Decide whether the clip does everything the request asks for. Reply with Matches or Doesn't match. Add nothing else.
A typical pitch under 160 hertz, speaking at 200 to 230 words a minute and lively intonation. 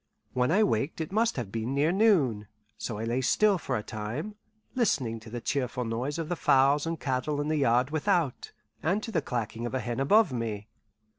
Matches